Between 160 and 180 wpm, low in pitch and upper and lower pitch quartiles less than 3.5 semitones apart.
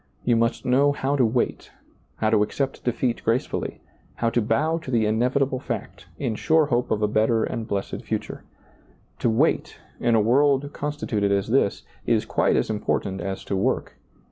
No: average, 175 wpm; low, 115 Hz; average, 3.8 semitones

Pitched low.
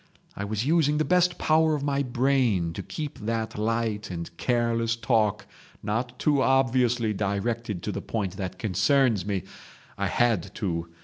Yes: low, 115 Hz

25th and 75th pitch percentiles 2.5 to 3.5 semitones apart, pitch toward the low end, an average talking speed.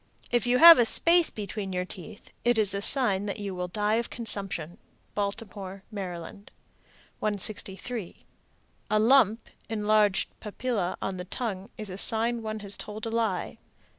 No: average, 2.8 semitones; high, 210 Hz; average, 155 wpm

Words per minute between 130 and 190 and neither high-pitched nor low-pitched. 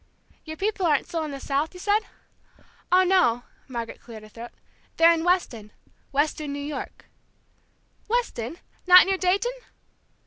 No: average, 145 wpm; very high, 315 Hz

